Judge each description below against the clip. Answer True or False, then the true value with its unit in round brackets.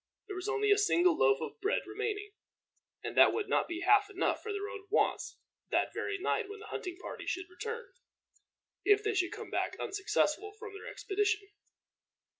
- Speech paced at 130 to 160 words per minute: False (185 wpm)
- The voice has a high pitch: True (410 Hz)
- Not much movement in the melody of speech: True (1.8 semitones)